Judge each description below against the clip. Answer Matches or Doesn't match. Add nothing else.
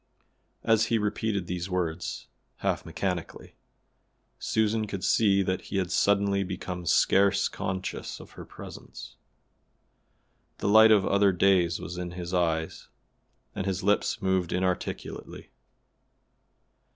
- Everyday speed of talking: Doesn't match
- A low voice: Matches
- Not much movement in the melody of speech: Matches